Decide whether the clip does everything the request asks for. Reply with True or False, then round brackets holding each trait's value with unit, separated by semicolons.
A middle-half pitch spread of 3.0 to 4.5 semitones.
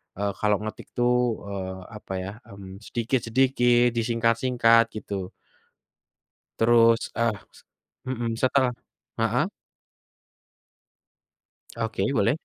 False (2.6 semitones)